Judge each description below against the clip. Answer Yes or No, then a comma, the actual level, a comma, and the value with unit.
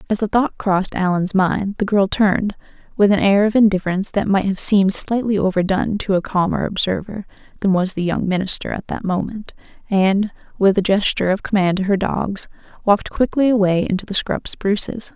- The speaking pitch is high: Yes, high, 195 Hz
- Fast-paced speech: No, average, 190 wpm